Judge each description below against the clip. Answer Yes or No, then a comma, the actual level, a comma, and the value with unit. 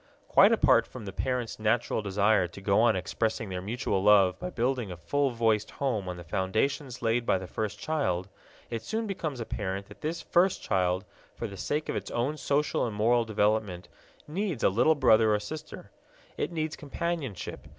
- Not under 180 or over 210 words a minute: Yes, average, 185 wpm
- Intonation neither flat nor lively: No, wide, 5.9 semitones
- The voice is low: Yes, low, 110 Hz